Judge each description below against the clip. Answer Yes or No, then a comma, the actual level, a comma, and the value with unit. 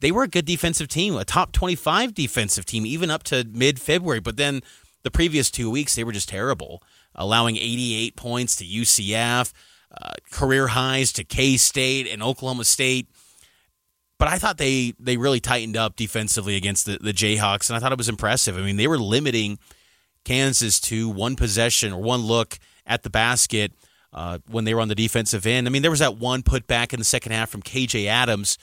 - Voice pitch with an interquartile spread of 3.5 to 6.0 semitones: No, average, 3.1 semitones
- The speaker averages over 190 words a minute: Yes, average, 200 wpm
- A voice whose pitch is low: Yes, low, 120 Hz